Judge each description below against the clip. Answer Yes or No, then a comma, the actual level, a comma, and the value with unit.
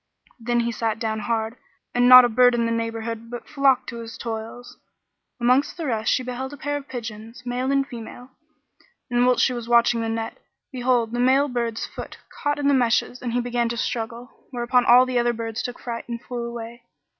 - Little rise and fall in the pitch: Yes, narrow, 1.5 semitones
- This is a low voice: No, high, 240 Hz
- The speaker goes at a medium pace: No, fast, 215 wpm